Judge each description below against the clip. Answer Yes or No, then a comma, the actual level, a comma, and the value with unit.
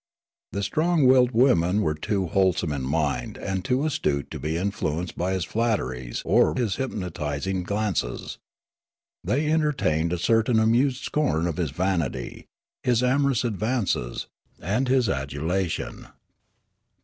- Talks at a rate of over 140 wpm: No, slow, 135 wpm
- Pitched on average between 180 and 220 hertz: No, very low, 95 Hz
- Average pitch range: No, wide, 7.7 semitones